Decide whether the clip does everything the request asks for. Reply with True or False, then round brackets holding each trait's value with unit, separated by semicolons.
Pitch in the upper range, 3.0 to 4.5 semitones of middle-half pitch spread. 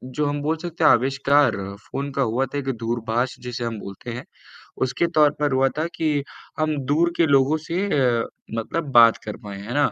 False (140 Hz; 4.0 semitones)